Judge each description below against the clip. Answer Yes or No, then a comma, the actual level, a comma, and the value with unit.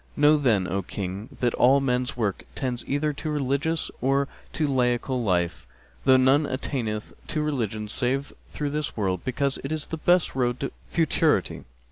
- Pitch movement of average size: Yes, average, 4.0 semitones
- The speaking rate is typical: Yes, average, 165 wpm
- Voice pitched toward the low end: Yes, low, 130 Hz